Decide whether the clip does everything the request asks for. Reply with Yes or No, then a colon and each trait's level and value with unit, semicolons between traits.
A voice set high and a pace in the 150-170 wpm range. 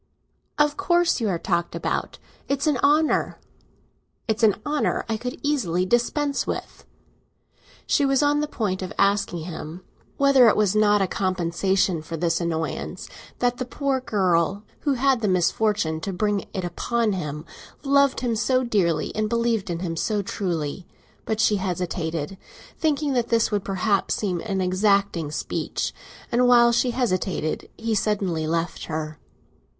Yes: high, 205 Hz; average, 155 wpm